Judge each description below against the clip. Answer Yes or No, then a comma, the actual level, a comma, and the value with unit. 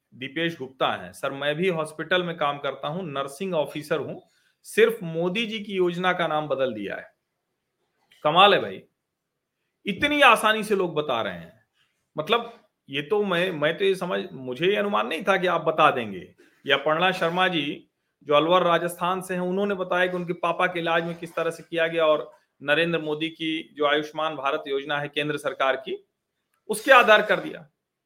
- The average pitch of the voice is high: No, medium, 170 Hz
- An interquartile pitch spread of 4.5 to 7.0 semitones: No, average, 3.8 semitones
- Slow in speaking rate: No, fast, 190 wpm